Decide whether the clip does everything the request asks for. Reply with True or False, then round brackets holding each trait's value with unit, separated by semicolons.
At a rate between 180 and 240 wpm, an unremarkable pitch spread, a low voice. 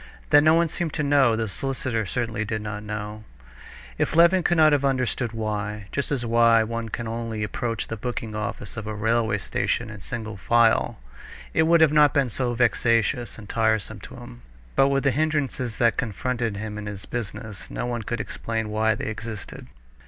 True (195 wpm; 3.1 semitones; 115 Hz)